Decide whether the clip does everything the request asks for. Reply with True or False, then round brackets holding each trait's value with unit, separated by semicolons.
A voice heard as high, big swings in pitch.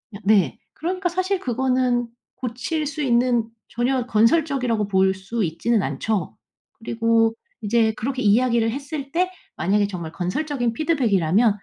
False (235 Hz; 4.3 semitones)